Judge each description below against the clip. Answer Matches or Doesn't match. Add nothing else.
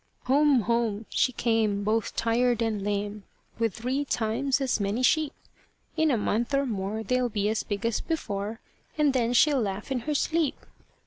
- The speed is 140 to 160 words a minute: Doesn't match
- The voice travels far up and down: Doesn't match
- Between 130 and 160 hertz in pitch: Doesn't match